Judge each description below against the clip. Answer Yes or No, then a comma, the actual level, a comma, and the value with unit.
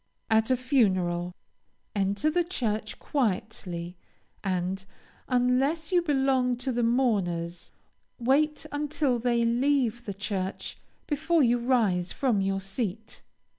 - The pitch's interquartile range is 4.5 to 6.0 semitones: Yes, wide, 5.6 semitones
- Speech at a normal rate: No, slow, 115 wpm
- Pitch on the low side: No, high, 235 Hz